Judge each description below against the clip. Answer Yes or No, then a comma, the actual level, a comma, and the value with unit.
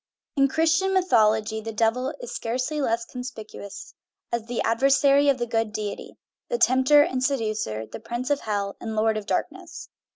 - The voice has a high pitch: Yes, high, 235 Hz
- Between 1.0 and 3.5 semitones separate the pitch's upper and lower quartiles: No, average, 4.1 semitones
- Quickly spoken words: No, average, 165 wpm